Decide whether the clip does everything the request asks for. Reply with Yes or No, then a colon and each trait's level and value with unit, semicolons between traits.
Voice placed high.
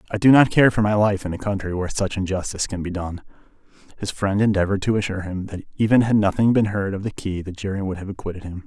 No: low, 100 Hz